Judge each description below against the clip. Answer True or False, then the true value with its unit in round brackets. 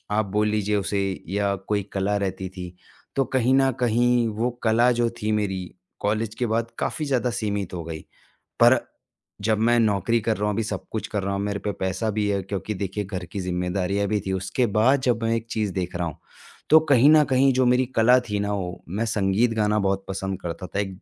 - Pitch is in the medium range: False (105 Hz)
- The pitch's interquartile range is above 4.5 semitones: False (3.1 semitones)